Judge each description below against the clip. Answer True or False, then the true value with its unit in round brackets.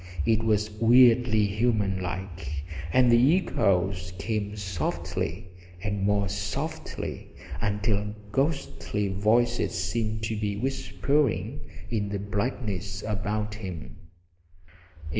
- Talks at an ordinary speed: False (100 wpm)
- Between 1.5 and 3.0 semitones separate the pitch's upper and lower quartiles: True (2.6 semitones)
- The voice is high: False (105 Hz)